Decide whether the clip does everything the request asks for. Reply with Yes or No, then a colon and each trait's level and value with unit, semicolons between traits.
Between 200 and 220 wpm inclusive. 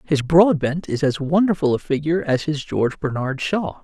No: average, 190 wpm